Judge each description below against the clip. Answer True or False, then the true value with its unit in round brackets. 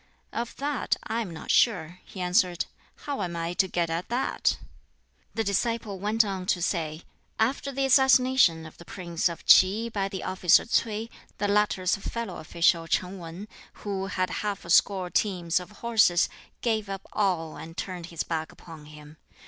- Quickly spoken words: False (175 wpm)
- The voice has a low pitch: False (190 Hz)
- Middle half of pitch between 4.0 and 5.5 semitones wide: True (4.4 semitones)